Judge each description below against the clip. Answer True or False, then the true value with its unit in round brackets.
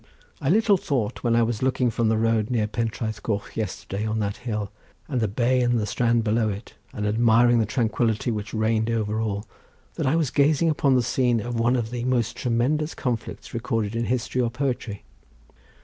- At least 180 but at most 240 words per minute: True (195 wpm)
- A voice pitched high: False (115 Hz)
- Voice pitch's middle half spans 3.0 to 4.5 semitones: False (2.4 semitones)